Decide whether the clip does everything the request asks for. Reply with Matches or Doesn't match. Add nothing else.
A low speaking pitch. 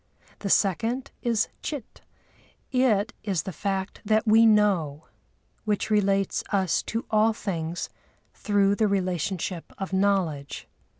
Doesn't match